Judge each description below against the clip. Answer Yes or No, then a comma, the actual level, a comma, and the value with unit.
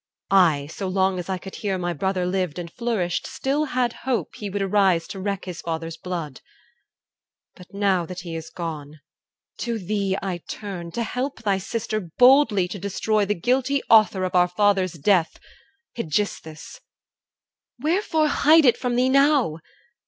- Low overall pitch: No, high, 195 Hz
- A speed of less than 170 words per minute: Yes, average, 160 wpm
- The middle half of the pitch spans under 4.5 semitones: No, average, 4.9 semitones